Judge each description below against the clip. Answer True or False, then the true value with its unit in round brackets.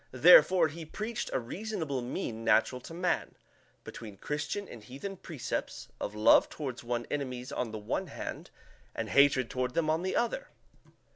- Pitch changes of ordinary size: False (6.2 semitones)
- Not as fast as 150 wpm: False (160 wpm)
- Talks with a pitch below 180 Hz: True (140 Hz)